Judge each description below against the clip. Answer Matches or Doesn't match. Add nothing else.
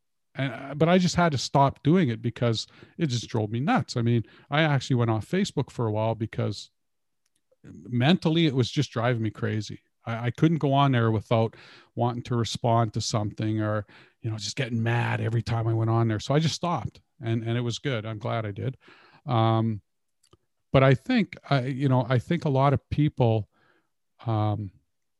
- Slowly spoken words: Doesn't match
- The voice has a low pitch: Matches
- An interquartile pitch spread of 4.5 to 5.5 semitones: Doesn't match